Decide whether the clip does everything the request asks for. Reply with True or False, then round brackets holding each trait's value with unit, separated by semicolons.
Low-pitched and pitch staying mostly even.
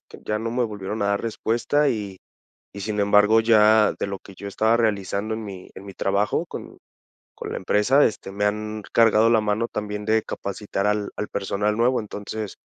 True (105 Hz; 1.6 semitones)